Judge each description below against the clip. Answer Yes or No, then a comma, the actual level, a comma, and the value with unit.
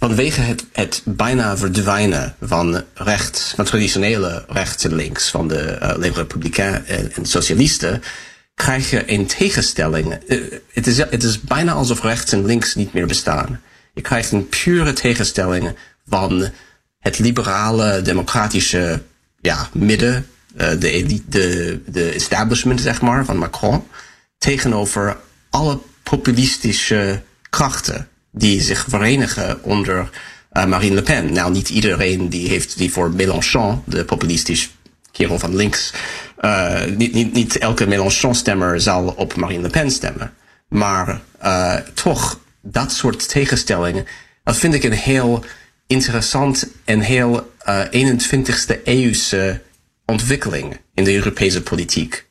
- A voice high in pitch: No, low, 105 Hz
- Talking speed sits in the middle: No, slow, 130 wpm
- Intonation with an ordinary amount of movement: Yes, average, 4.5 semitones